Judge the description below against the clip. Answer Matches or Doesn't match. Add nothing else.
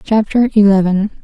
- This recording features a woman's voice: Matches